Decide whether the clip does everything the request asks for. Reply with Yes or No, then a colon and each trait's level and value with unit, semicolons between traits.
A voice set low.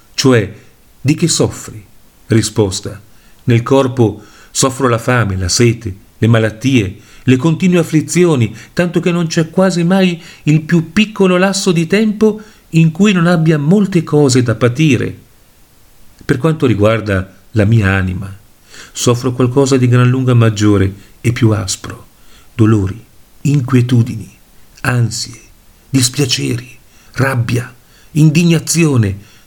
Yes: low, 125 Hz